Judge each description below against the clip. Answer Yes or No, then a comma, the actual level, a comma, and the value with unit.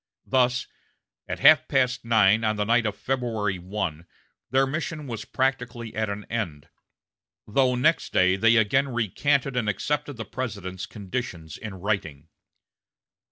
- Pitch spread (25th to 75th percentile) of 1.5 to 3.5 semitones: No, average, 4.3 semitones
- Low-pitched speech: Yes, low, 115 Hz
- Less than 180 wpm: Yes, average, 140 wpm